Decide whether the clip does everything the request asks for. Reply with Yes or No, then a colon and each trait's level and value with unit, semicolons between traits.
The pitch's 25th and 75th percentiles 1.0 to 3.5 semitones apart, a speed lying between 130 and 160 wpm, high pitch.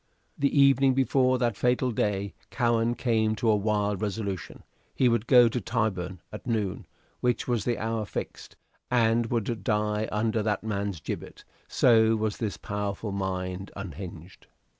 No: average, 2.8 semitones; average, 150 wpm; low, 110 Hz